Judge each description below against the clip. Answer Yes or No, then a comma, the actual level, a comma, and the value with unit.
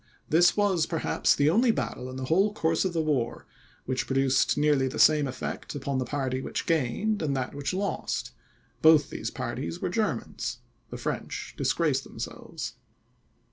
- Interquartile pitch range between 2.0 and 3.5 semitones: No, average, 4.2 semitones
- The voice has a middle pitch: Yes, medium, 150 Hz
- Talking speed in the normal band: Yes, average, 165 wpm